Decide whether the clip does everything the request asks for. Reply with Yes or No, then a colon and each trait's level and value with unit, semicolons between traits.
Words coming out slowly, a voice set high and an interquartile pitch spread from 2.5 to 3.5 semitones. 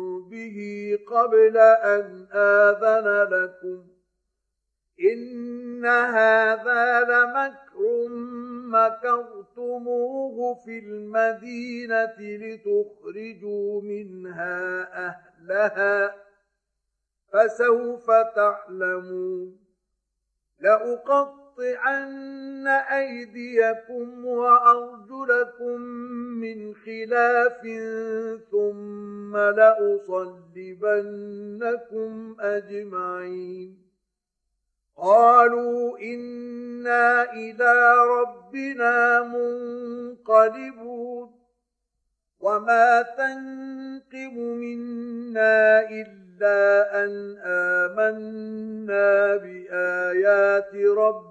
Yes: slow, 45 wpm; high, 225 Hz; average, 2.9 semitones